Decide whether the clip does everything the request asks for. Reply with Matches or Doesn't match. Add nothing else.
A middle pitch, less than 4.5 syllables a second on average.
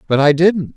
Doesn't match